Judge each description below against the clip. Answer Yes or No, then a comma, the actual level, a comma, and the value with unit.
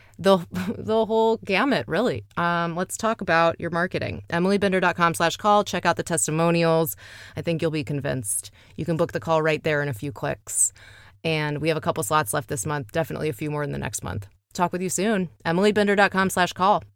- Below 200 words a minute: No, fast, 205 wpm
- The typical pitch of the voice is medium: Yes, medium, 165 Hz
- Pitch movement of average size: Yes, average, 3.8 semitones